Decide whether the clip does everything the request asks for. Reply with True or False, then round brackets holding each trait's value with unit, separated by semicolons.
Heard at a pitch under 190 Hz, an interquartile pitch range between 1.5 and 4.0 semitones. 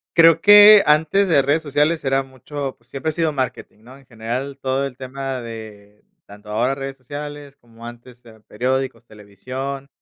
True (135 Hz; 3.6 semitones)